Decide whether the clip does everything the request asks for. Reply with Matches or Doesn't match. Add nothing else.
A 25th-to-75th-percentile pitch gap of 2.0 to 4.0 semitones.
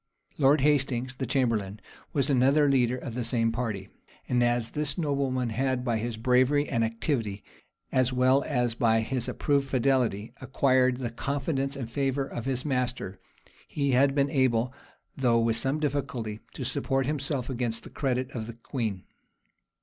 Matches